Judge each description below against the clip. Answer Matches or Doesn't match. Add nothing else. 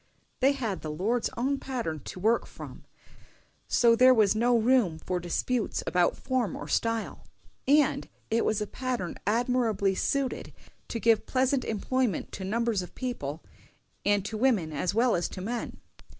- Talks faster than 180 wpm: Doesn't match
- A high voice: Matches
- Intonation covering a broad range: Doesn't match